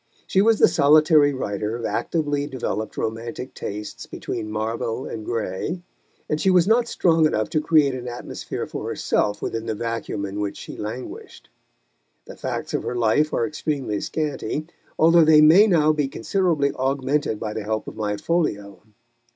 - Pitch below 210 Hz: Yes, low, 135 Hz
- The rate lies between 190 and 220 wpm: No, average, 165 wpm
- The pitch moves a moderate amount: No, wide, 6.0 semitones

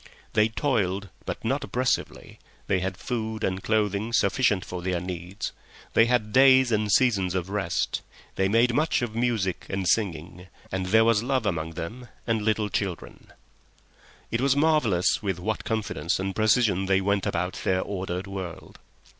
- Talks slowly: No, average, 160 wpm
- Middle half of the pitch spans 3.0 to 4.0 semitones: Yes, average, 3.6 semitones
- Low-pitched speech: Yes, low, 100 Hz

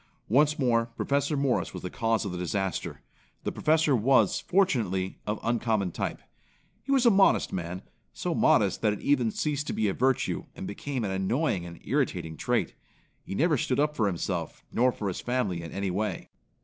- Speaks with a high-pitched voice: No, low, 115 Hz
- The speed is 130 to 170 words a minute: No, average, 190 wpm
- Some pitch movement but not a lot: No, wide, 6.7 semitones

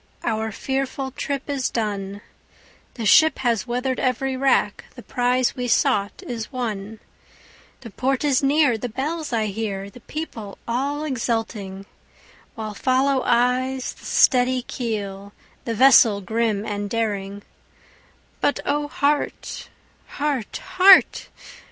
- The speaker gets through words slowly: Yes, slow, 125 wpm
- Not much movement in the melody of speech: No, average, 3.9 semitones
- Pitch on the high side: Yes, high, 245 Hz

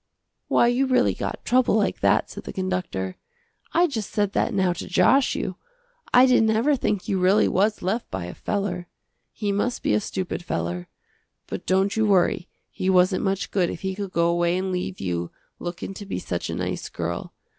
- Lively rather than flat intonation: No, average, 3.2 semitones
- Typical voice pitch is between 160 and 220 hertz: Yes, high, 190 Hz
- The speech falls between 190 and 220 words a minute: Yes, average, 200 wpm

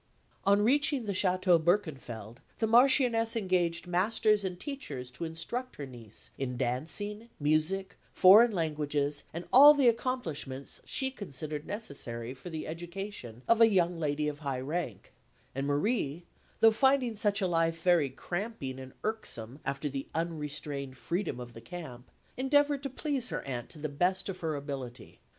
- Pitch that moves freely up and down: Yes, wide, 7.3 semitones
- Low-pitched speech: No, medium, 170 Hz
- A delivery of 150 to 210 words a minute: Yes, average, 155 wpm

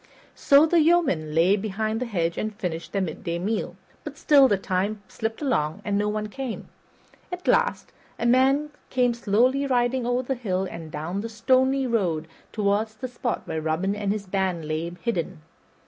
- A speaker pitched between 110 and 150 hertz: No, high, 215 Hz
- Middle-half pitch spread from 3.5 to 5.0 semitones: No, wide, 5.5 semitones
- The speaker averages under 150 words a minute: No, average, 180 wpm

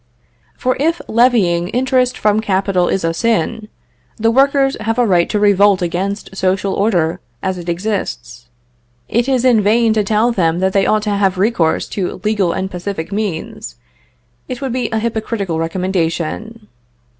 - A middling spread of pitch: Yes, average, 3.9 semitones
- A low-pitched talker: No, high, 205 Hz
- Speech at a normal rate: Yes, average, 160 wpm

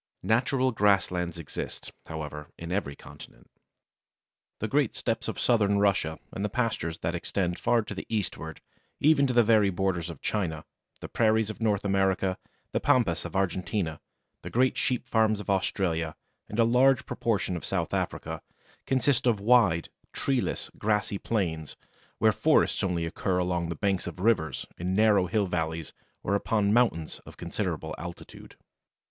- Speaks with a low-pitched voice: Yes, low, 100 Hz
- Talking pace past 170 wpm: No, average, 155 wpm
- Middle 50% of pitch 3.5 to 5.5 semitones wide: Yes, average, 4.7 semitones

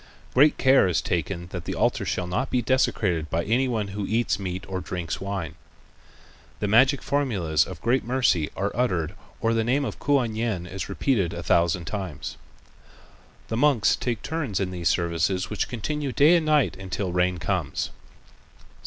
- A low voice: Yes, low, 100 Hz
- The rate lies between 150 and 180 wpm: Yes, average, 170 wpm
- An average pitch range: No, wide, 6.1 semitones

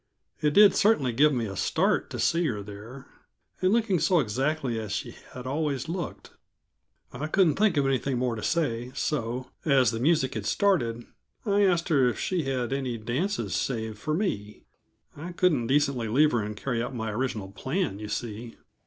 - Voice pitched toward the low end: Yes, low, 130 Hz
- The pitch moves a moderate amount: No, wide, 5.7 semitones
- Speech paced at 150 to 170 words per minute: No, average, 185 wpm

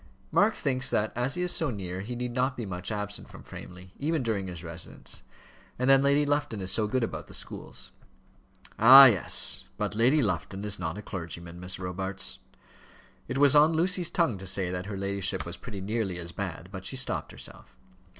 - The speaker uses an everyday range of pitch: No, wide, 6.1 semitones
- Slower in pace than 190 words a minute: No, average, 200 wpm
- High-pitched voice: No, low, 105 Hz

